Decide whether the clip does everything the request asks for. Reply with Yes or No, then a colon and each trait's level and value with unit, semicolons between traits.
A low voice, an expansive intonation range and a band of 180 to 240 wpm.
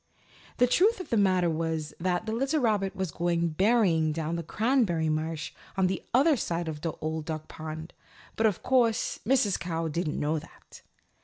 No: medium, 175 Hz; wide, 5.7 semitones; average, 185 wpm